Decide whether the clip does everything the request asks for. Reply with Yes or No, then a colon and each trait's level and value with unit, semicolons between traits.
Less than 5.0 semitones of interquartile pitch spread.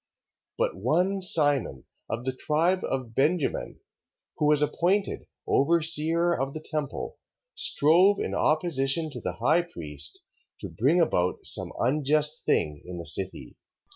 No: wide, 5.4 semitones